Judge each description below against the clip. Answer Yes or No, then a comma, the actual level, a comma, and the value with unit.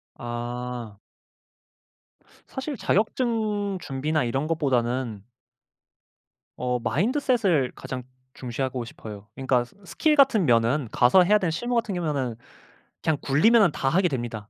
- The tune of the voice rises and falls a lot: Yes, wide, 8.6 semitones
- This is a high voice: No, medium, 140 Hz